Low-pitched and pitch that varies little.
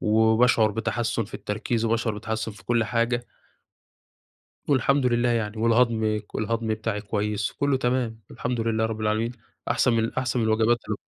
Yes: low, 115 Hz; narrow, 1.6 semitones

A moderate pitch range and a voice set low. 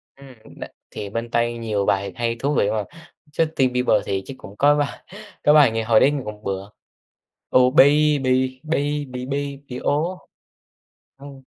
Yes: average, 4.2 semitones; low, 130 Hz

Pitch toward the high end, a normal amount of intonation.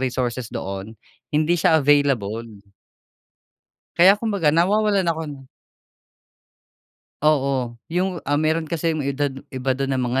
No: medium, 145 Hz; average, 4.2 semitones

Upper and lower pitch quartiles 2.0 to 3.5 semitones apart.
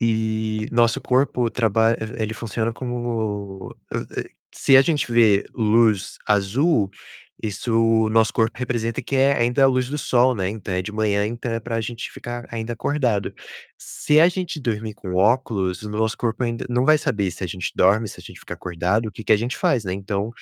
Yes: narrow, 2.5 semitones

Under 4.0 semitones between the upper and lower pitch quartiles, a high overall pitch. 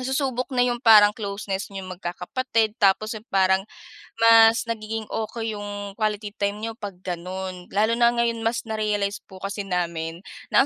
Yes: average, 2.8 semitones; high, 210 Hz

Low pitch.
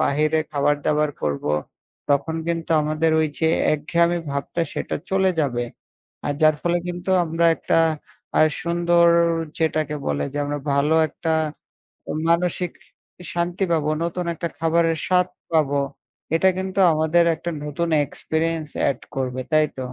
No: medium, 160 Hz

